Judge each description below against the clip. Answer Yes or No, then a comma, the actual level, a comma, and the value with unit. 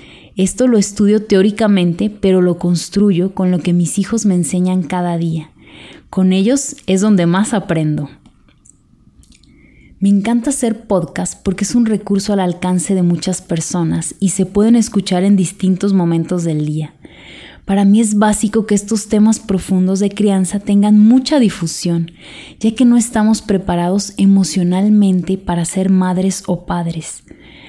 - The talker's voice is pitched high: Yes, high, 195 Hz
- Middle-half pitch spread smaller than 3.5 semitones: Yes, average, 2.8 semitones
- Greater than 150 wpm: No, average, 145 wpm